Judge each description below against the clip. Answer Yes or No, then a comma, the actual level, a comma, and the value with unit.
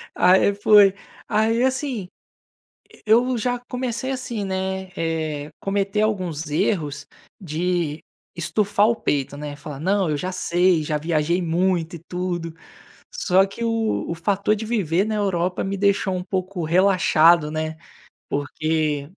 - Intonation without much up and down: No, average, 4.3 semitones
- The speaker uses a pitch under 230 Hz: Yes, medium, 185 Hz